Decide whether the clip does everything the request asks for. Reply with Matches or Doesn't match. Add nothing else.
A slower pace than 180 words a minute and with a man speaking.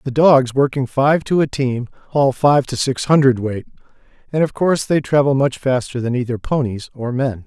Doesn't match